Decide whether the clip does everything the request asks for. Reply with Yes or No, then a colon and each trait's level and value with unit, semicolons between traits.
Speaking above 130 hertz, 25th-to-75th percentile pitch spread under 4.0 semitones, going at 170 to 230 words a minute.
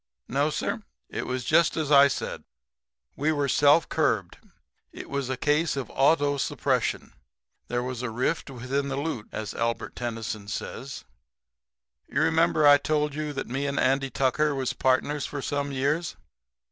No: medium, 140 Hz; narrow, 2.5 semitones; average, 160 wpm